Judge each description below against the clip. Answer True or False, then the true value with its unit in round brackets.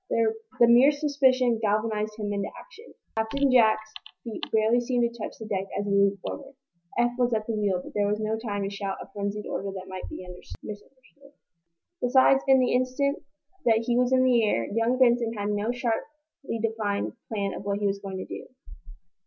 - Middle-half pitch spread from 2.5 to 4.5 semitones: True (3.5 semitones)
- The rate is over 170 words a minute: True (195 wpm)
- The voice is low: False (225 Hz)